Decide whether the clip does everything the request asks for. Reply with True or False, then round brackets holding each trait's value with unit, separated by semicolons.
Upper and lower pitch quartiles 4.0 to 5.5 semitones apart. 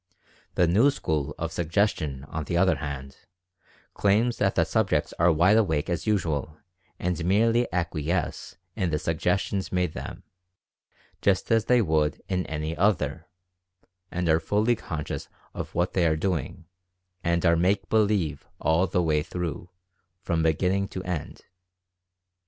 False (3.6 semitones)